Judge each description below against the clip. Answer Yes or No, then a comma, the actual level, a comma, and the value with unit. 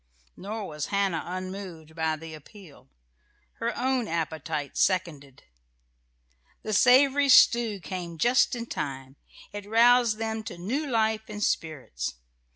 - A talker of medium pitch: No, high, 195 Hz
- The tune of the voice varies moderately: No, wide, 6.2 semitones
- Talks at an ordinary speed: No, slow, 125 wpm